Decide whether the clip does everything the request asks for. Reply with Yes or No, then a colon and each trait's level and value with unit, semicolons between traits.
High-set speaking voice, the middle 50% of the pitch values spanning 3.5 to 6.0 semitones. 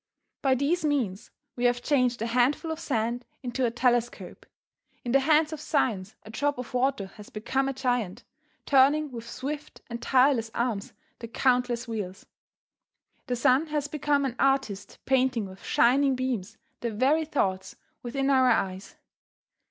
No: very high, 250 Hz; average, 3.1 semitones